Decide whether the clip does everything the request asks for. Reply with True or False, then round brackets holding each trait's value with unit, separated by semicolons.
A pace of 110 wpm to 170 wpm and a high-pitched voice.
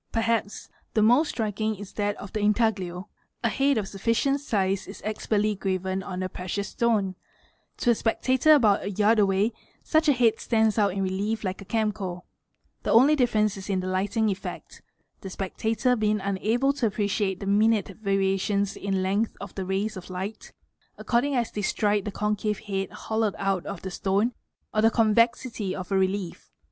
False (180 wpm; 205 Hz)